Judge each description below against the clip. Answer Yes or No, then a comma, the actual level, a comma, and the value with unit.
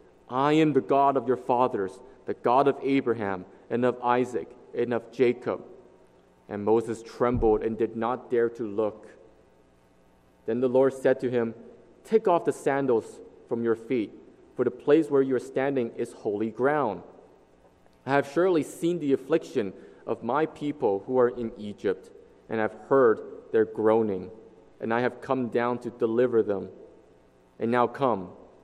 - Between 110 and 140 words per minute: No, average, 165 wpm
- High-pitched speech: No, low, 125 Hz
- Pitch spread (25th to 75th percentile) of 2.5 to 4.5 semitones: Yes, average, 3.6 semitones